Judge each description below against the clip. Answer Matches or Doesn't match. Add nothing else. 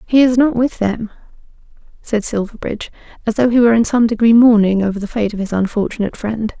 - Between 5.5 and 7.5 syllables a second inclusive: Matches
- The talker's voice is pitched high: Matches